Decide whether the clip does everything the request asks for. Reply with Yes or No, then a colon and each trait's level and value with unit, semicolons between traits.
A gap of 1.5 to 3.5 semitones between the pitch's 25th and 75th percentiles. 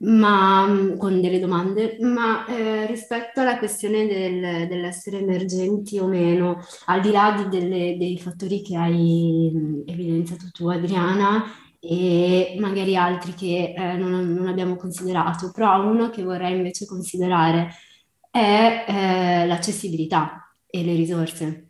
Yes: narrow, 2.5 semitones